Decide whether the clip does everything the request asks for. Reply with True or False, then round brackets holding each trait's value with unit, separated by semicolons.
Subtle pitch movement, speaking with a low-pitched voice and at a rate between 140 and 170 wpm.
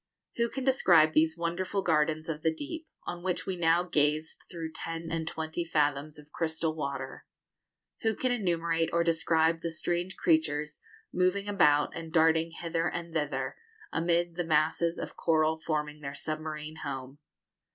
False (1.9 semitones; 165 Hz; 155 wpm)